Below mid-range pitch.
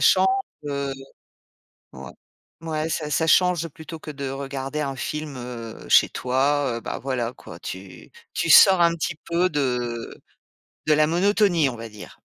No: medium, 145 Hz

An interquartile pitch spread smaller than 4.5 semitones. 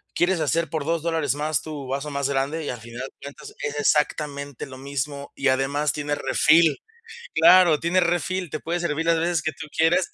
Yes: average, 2.8 semitones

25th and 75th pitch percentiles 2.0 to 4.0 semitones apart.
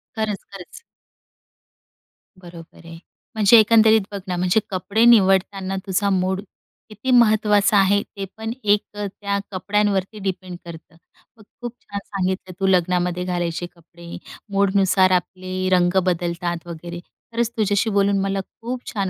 Yes: narrow, 2.4 semitones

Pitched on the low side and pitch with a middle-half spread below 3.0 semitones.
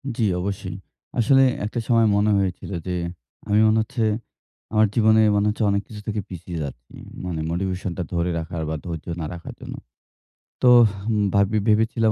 No: low, 100 Hz; average, 3.6 semitones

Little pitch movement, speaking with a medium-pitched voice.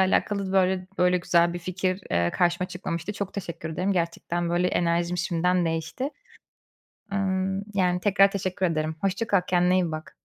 Yes: narrow, 1.8 semitones; medium, 180 Hz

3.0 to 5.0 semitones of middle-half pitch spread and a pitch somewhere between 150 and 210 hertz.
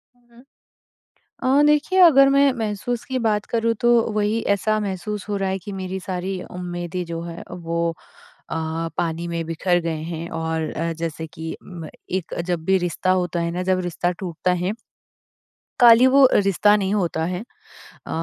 Yes: average, 4.1 semitones; medium, 185 Hz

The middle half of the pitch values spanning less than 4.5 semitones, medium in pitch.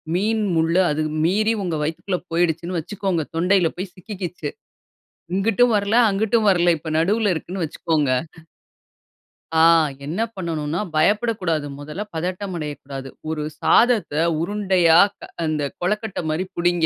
Yes: average, 4.0 semitones; medium, 175 Hz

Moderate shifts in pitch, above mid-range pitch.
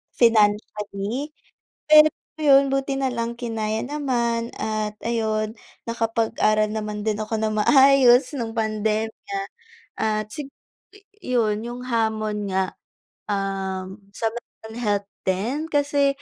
Yes: average, 3.3 semitones; high, 225 Hz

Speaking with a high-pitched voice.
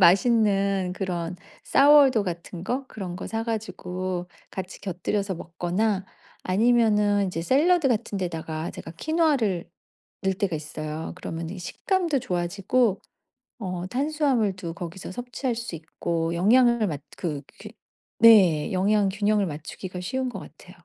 Yes: high, 195 Hz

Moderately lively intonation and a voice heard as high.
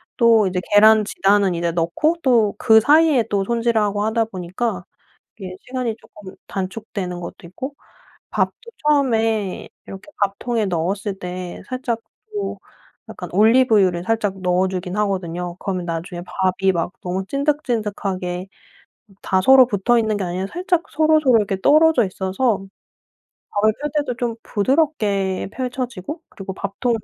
Yes: average, 4.6 semitones; high, 205 Hz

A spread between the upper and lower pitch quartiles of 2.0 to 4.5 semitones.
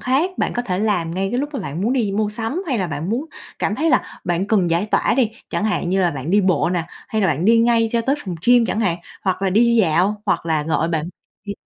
No: average, 5.0 semitones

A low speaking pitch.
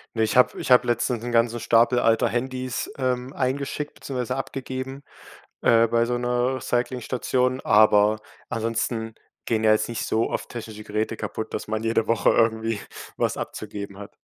Yes: low, 115 Hz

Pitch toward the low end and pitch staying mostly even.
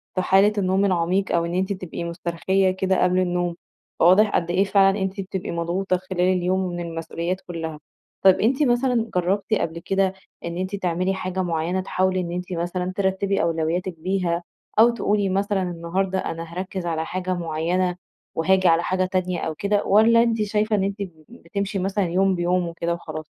No: medium, 185 Hz; narrow, 2.2 semitones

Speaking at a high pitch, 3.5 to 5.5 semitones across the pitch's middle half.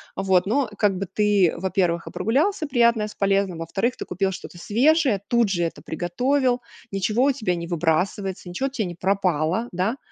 Yes: high, 195 Hz; average, 4.8 semitones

